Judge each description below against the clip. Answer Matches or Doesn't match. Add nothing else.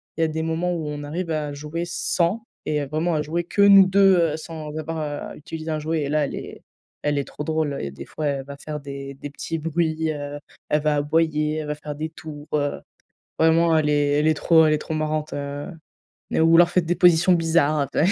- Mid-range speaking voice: Matches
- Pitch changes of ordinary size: Doesn't match